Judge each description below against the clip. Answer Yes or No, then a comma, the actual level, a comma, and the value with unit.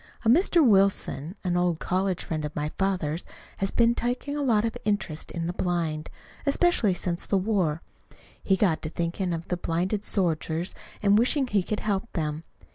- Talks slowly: No, average, 180 wpm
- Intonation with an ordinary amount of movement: Yes, average, 4.2 semitones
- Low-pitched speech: No, medium, 185 Hz